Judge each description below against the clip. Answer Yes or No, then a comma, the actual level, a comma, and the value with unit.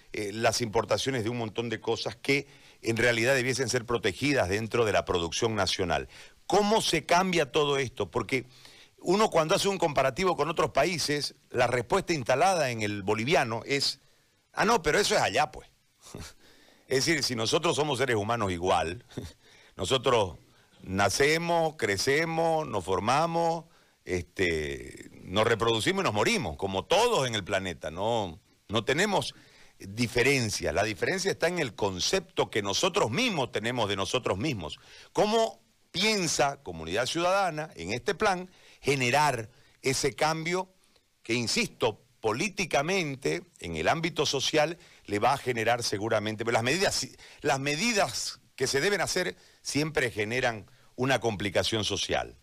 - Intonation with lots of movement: Yes, wide, 6.3 semitones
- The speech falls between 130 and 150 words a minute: Yes, average, 140 wpm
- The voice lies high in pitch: No, low, 135 Hz